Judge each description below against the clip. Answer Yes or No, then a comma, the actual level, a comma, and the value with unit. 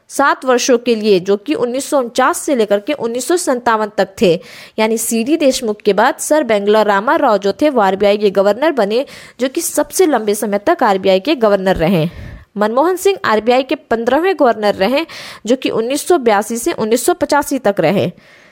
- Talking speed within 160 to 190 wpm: No, average, 150 wpm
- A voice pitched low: No, high, 235 Hz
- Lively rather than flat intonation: Yes, wide, 6.1 semitones